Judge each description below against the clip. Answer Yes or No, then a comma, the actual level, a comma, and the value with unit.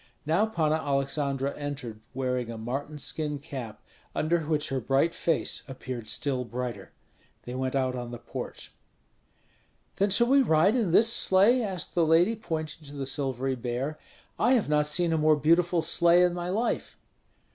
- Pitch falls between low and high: Yes, medium, 150 Hz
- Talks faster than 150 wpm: Yes, average, 170 wpm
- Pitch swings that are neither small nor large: Yes, average, 4.7 semitones